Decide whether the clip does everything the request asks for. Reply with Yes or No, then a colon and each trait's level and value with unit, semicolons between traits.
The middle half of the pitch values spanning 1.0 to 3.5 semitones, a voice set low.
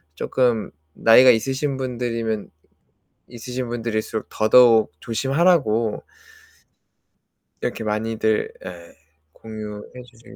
Yes: narrow, 2.5 semitones; low, 115 Hz